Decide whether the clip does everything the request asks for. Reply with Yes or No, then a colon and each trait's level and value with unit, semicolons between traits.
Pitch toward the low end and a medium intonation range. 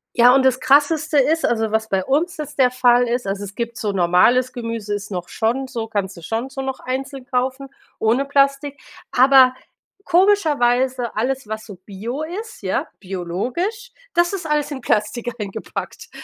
No: very high, 250 Hz; average, 4.1 semitones